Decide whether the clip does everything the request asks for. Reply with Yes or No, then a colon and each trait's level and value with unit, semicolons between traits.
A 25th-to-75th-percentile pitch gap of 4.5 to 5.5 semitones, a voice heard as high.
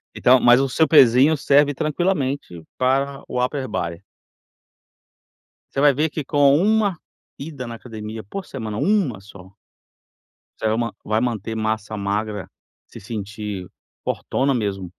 No: average, 5.0 semitones; low, 125 Hz